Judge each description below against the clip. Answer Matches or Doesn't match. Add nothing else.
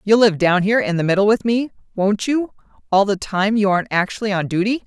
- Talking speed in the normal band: Doesn't match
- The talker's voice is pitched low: Doesn't match